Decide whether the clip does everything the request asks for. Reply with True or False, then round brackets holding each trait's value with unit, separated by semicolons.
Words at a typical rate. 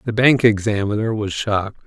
True (160 wpm)